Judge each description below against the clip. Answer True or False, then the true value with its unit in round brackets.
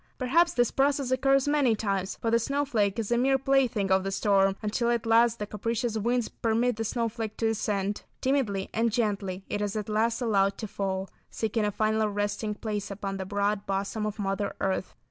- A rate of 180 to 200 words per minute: True (195 wpm)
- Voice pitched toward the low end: False (215 Hz)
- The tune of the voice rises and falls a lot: False (2.9 semitones)